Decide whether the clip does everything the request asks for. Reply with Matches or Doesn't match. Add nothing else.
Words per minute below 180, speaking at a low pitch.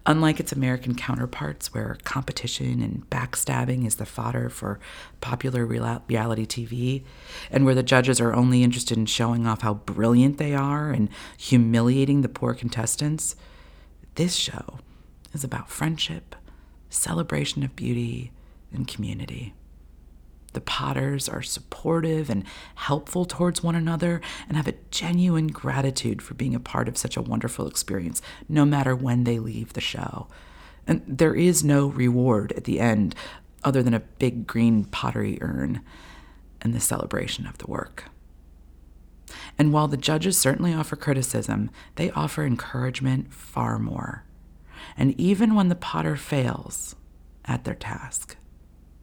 Matches